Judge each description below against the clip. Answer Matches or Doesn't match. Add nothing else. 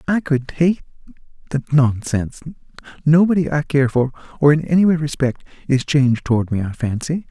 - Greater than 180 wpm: Doesn't match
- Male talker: Matches